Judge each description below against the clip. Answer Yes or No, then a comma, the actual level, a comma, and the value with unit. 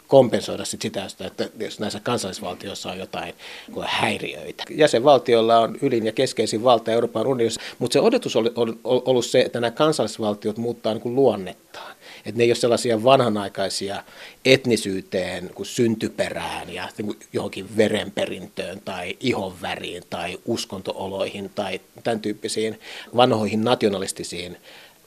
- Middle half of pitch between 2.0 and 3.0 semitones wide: Yes, narrow, 2.4 semitones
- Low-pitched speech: Yes, low, 115 Hz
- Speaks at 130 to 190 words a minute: No, average, 115 wpm